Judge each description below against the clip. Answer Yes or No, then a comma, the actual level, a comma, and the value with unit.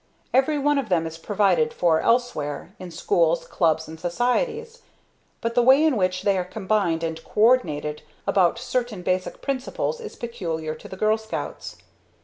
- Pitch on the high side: Yes, high, 195 Hz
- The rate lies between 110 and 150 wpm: No, average, 165 wpm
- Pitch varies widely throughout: Yes, wide, 6.9 semitones